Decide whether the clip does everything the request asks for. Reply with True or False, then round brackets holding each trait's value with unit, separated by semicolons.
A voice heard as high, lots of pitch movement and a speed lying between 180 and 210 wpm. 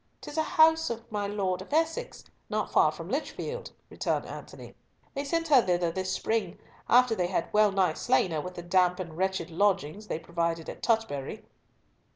True (195 Hz; 5.7 semitones; 185 wpm)